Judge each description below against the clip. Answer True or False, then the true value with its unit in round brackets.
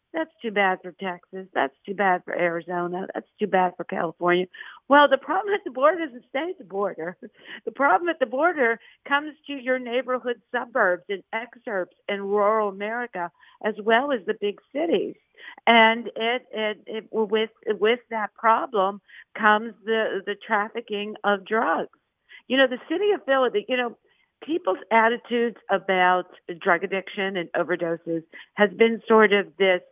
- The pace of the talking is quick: False (160 wpm)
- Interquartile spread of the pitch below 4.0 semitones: False (4.4 semitones)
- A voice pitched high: True (215 Hz)